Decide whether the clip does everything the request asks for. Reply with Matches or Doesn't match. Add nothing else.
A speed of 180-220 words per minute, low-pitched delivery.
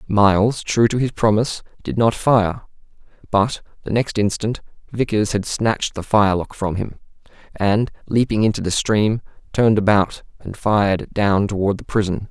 Doesn't match